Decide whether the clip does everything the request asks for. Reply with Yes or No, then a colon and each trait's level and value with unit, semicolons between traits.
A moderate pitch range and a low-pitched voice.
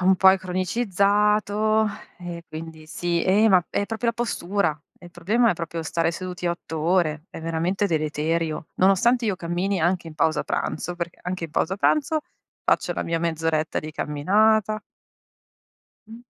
No: average, 3.8 semitones; medium, 175 Hz